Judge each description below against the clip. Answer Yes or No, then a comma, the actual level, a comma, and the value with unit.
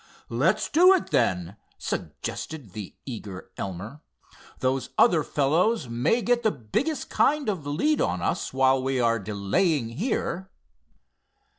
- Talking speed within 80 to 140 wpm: Yes, slow, 135 wpm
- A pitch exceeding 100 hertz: Yes, low, 135 Hz